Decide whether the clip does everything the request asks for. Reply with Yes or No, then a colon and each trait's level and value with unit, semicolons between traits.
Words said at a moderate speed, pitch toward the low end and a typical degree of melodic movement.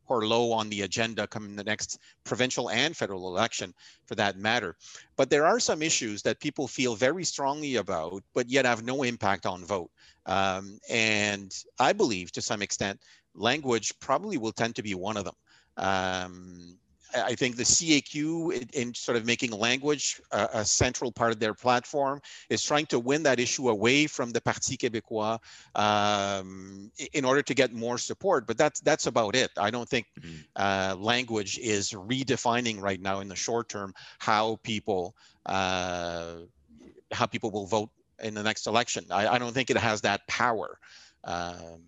Yes: average, 175 wpm; low, 110 Hz; average, 4.1 semitones